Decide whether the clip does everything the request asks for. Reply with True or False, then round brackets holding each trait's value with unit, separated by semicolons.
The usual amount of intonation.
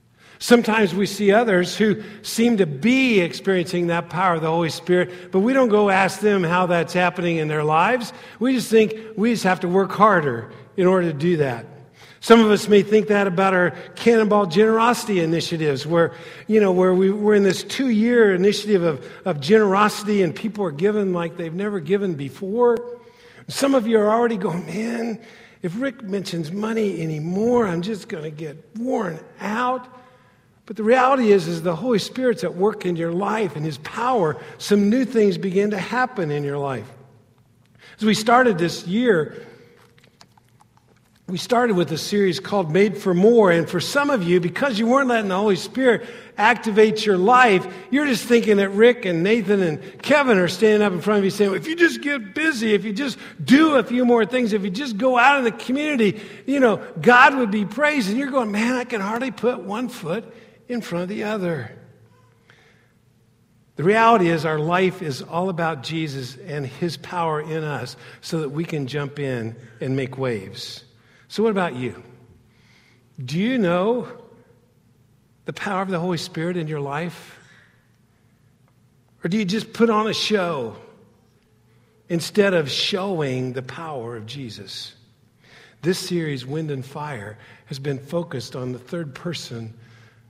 False (5.9 semitones)